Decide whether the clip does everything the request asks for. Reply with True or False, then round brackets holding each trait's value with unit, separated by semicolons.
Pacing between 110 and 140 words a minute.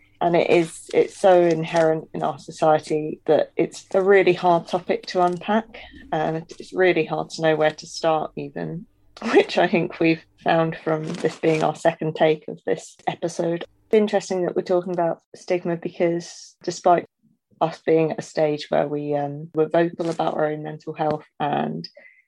False (180 wpm)